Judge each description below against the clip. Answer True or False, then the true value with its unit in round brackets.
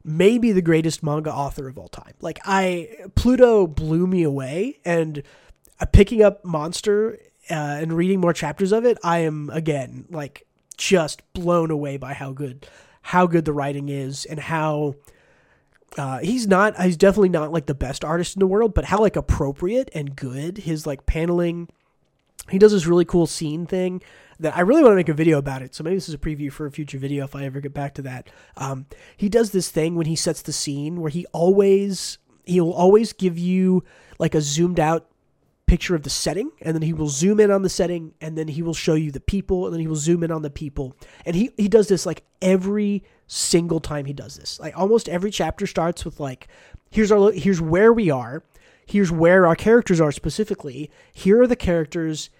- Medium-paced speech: False (210 wpm)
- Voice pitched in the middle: True (165 Hz)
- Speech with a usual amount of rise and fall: True (4.1 semitones)